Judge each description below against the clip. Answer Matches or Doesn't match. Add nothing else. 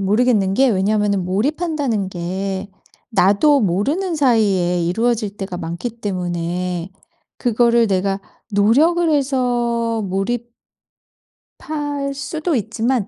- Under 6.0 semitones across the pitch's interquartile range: Matches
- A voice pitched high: Matches